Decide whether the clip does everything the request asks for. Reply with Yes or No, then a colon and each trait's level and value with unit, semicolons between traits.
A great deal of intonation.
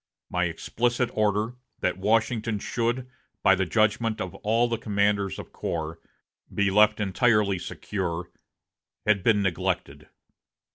No: average, 3.0 semitones